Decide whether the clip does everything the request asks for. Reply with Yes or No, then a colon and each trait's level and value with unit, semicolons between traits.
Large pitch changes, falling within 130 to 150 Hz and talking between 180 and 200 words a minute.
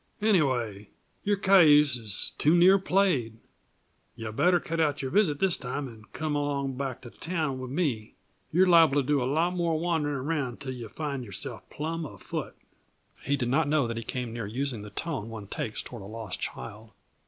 Yes: wide, 5.8 semitones; medium, 140 Hz; average, 190 wpm